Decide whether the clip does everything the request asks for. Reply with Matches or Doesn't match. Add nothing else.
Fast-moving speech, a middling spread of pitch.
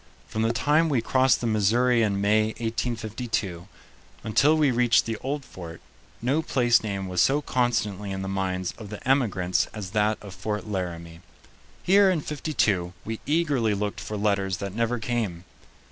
Doesn't match